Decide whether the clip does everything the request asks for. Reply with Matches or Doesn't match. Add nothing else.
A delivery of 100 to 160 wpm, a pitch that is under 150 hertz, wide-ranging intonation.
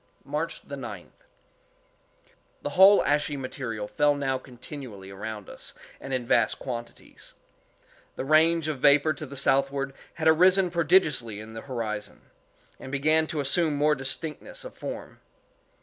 Doesn't match